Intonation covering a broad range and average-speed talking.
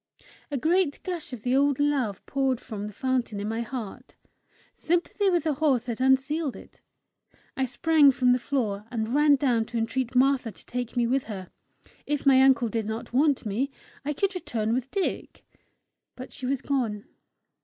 No: average, 3.6 semitones; average, 180 wpm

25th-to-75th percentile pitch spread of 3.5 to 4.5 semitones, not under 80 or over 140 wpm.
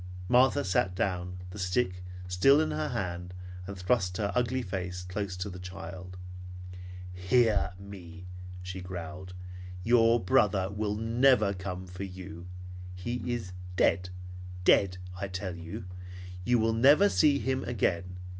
Yes: average, 3.8 semitones; slow, 135 wpm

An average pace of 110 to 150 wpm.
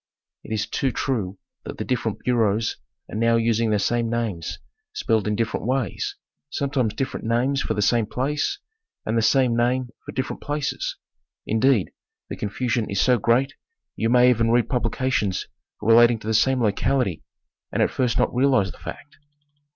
No: average, 170 wpm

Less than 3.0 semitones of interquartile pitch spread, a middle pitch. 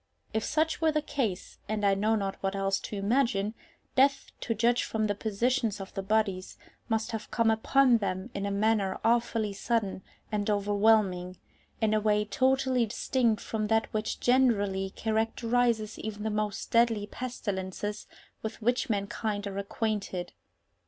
No: narrow, 2.6 semitones; high, 215 Hz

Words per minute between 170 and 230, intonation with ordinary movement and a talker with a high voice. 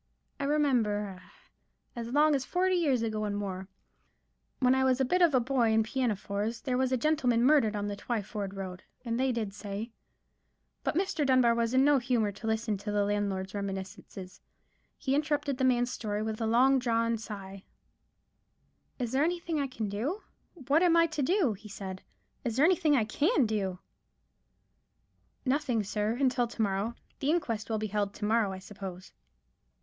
Yes: average, 175 wpm; average, 4.7 semitones; high, 230 Hz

